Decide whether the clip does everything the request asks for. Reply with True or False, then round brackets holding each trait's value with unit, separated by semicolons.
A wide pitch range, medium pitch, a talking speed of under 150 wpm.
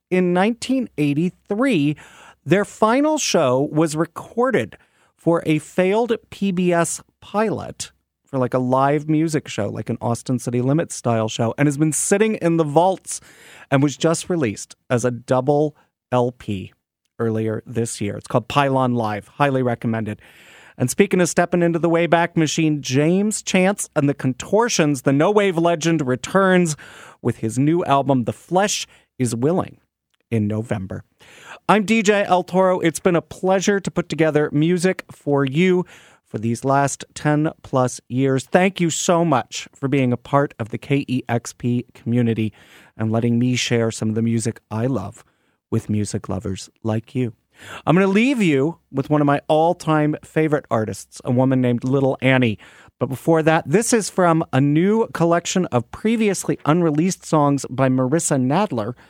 False (5.8 semitones; 145 Hz; 160 wpm)